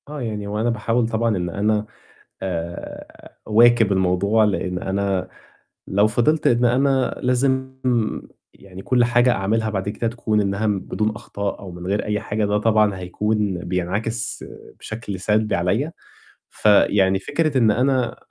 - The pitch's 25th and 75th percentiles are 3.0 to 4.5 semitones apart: Yes, average, 3.4 semitones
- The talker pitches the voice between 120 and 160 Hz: No, low, 105 Hz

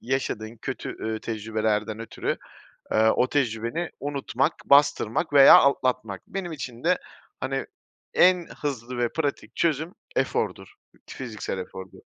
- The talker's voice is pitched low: Yes, low, 125 Hz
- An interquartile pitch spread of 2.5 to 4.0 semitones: No, average, 4.5 semitones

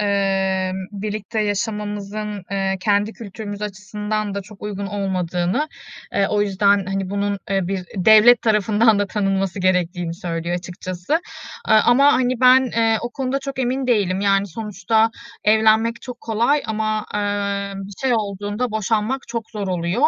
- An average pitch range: No, narrow, 2.2 semitones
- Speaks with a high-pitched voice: Yes, high, 205 Hz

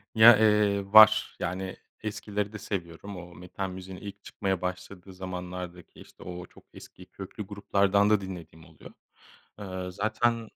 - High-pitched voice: No, very low, 95 Hz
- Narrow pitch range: Yes, narrow, 2.2 semitones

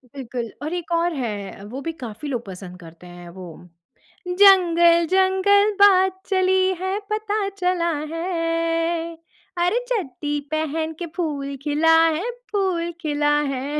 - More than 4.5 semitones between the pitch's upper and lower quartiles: Yes, average, 5.1 semitones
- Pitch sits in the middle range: No, very high, 330 Hz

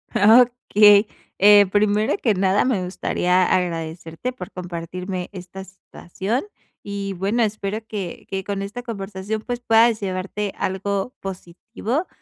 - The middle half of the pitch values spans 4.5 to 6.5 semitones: No, average, 2.7 semitones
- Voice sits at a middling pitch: No, high, 200 Hz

